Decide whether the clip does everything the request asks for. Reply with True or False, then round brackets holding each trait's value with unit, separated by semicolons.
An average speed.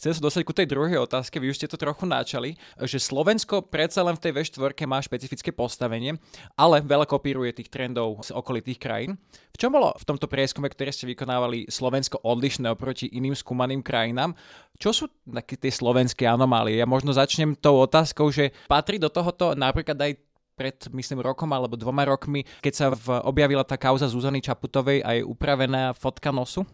False (185 wpm)